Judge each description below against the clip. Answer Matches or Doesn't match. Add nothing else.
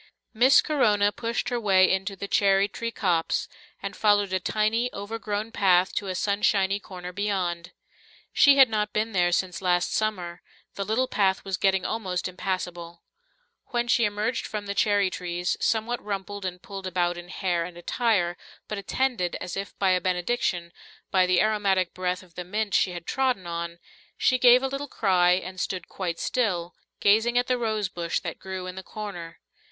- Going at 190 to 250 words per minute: Doesn't match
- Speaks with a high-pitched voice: Matches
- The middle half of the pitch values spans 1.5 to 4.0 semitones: Matches